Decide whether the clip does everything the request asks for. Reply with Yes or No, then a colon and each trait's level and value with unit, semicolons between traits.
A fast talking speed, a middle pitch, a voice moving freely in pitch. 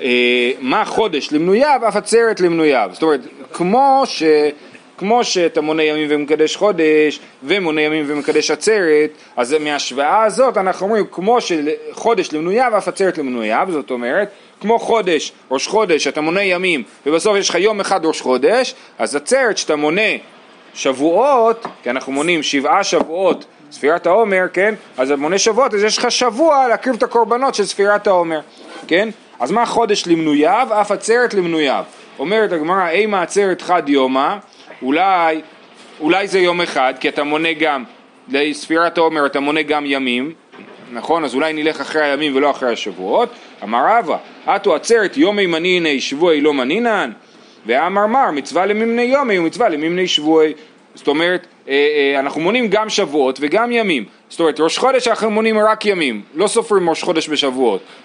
Yes: fast, 155 wpm; medium, 175 Hz; wide, 6.2 semitones